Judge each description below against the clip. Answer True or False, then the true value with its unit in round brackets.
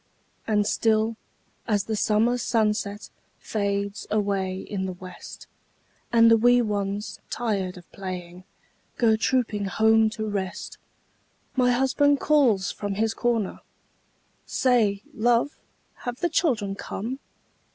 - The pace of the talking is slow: True (120 wpm)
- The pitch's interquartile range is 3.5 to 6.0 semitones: False (3.0 semitones)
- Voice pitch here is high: True (215 Hz)